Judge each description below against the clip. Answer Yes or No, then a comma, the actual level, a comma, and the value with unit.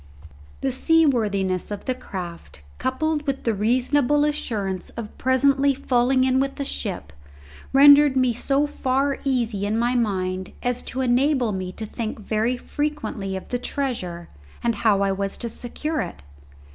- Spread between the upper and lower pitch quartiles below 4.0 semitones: No, average, 5.1 semitones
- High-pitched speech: Yes, high, 245 Hz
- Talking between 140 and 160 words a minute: Yes, average, 155 wpm